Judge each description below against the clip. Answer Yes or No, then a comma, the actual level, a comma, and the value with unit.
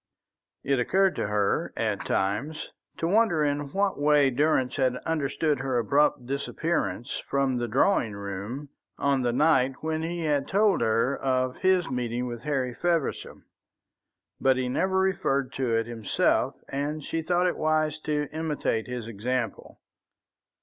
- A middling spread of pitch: Yes, average, 4.2 semitones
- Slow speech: No, average, 150 wpm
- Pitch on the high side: No, medium, 140 Hz